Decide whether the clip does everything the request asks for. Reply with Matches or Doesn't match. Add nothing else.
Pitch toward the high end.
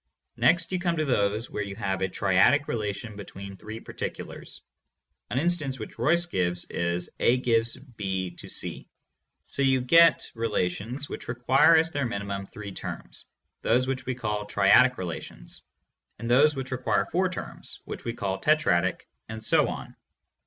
Doesn't match